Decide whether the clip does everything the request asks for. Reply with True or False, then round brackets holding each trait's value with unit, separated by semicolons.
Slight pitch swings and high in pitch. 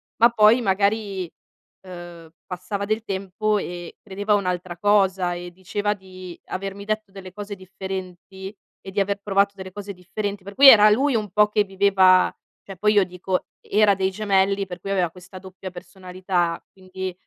True (1.9 semitones; 195 Hz)